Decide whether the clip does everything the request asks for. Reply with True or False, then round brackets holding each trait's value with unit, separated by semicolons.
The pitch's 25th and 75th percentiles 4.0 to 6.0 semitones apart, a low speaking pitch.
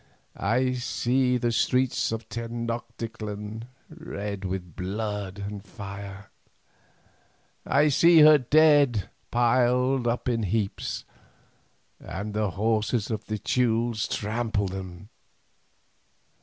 False (3.3 semitones; 115 Hz)